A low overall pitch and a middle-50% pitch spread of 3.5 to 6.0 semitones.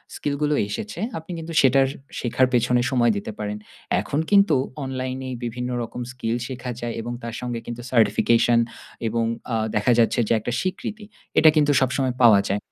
No: low, 125 Hz; average, 2.7 semitones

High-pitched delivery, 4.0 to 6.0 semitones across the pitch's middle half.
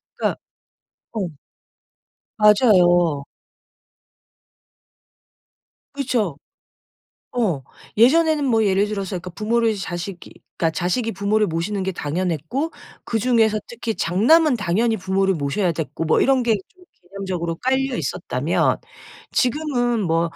Yes: high, 205 Hz; wide, 5.4 semitones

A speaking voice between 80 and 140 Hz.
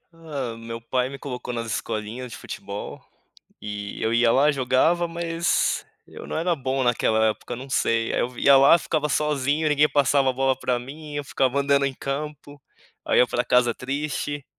Yes: low, 135 Hz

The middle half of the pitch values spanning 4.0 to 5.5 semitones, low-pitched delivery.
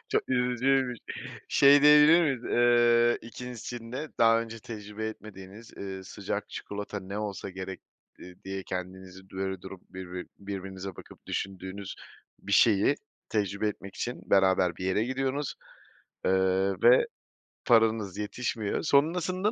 Yes: average, 4.4 semitones; low, 105 Hz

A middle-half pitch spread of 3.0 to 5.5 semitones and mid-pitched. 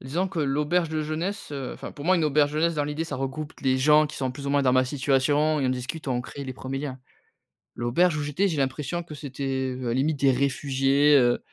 No: narrow, 2.6 semitones; medium, 145 Hz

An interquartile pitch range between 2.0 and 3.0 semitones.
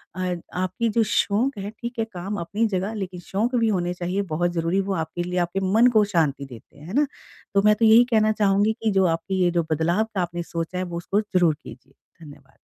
No: average, 3.4 semitones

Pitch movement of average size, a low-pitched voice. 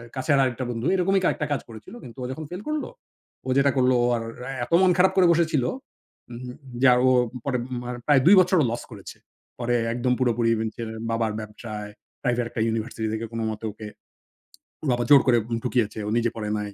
Yes: average, 3.6 semitones; low, 120 Hz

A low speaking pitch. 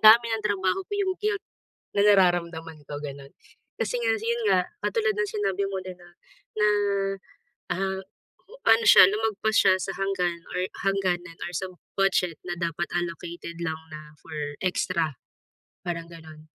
No: medium, 185 Hz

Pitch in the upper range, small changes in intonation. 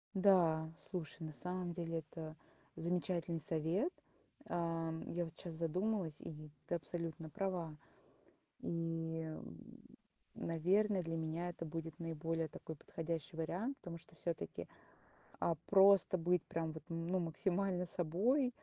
No: medium, 165 Hz; narrow, 1.9 semitones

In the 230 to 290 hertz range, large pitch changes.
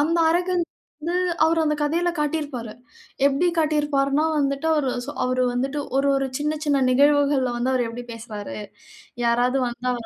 No: very high, 280 Hz; average, 3.2 semitones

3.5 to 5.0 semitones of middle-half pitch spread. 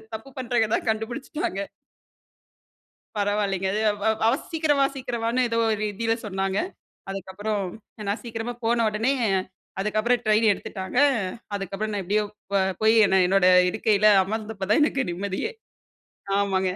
No: average, 2.8 semitones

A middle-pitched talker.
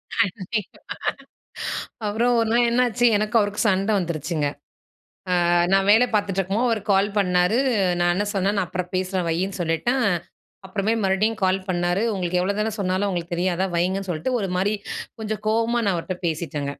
No: high, 195 Hz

